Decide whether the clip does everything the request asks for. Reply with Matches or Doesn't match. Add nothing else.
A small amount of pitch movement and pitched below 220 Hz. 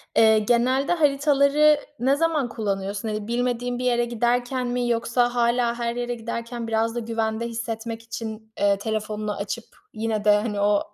Doesn't match